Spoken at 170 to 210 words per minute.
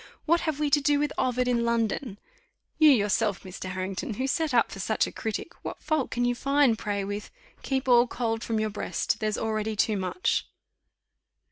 Yes: average, 195 wpm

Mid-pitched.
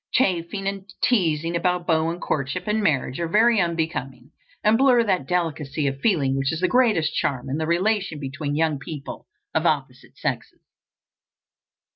Yes: medium, 165 Hz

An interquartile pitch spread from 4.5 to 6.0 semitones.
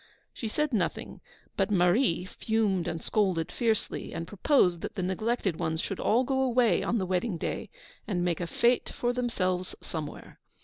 Yes: average, 5.0 semitones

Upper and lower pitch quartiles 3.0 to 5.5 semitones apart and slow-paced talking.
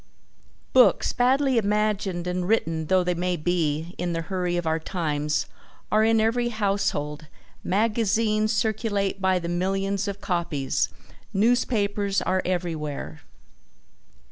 Yes: average, 3.9 semitones; slow, 120 wpm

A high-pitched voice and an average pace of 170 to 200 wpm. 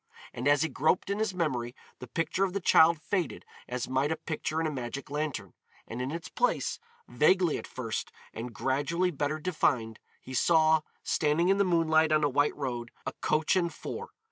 No: medium, 155 Hz; average, 195 wpm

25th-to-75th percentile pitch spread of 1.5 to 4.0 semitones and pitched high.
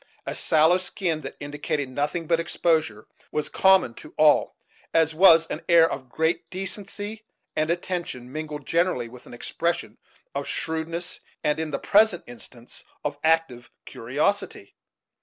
No: average, 2.9 semitones; medium, 160 Hz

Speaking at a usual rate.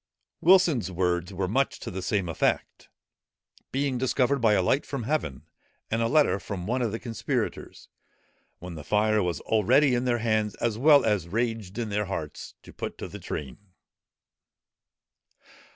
Yes: average, 165 wpm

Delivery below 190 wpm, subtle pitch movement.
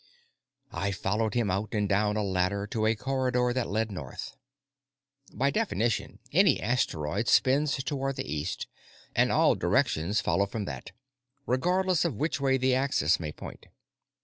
No: average, 150 wpm; average, 5.1 semitones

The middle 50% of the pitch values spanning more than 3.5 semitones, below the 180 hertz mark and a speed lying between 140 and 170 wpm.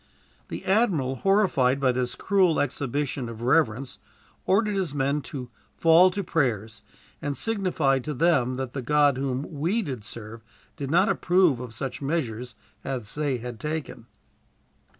Yes: average, 4.8 semitones; medium, 140 Hz; average, 150 wpm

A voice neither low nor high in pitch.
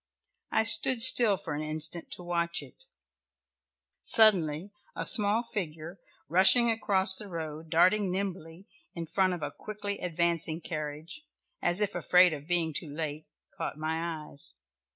Yes: medium, 175 Hz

